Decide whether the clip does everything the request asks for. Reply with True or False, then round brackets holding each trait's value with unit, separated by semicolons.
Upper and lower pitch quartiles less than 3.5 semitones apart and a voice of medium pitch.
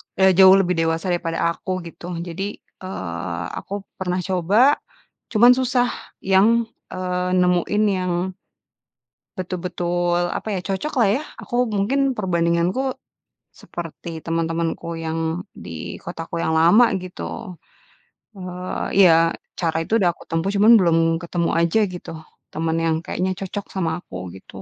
True (2.6 semitones; 180 Hz)